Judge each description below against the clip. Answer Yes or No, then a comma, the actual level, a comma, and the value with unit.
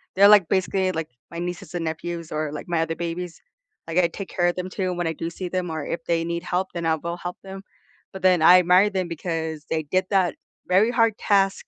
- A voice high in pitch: No, medium, 175 Hz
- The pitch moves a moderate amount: No, narrow, 2.1 semitones